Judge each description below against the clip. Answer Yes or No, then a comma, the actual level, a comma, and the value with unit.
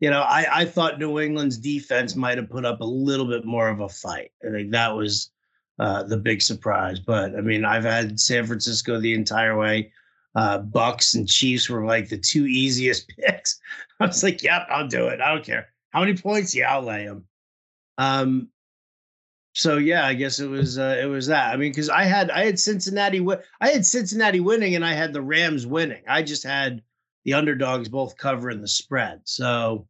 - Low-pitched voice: Yes, low, 130 Hz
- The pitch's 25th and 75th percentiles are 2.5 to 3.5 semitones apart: No, wide, 5.4 semitones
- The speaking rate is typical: No, fast, 210 wpm